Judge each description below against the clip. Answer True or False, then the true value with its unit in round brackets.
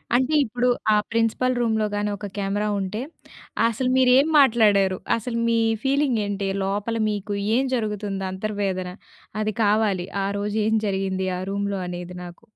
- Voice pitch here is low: False (210 Hz)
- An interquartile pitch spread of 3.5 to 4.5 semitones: False (2.9 semitones)